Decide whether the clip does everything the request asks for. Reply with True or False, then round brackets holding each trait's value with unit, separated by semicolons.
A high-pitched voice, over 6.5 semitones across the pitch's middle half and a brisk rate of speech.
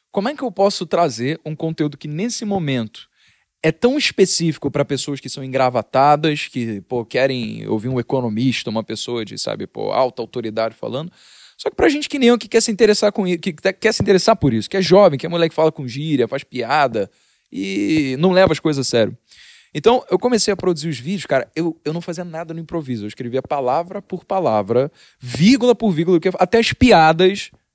False (160 Hz; 6.9 semitones; 210 wpm)